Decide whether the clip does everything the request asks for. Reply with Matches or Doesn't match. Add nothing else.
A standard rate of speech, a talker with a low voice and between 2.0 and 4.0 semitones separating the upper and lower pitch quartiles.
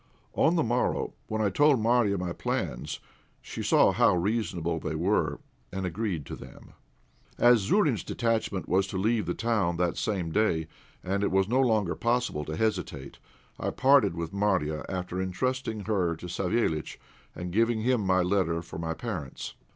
Doesn't match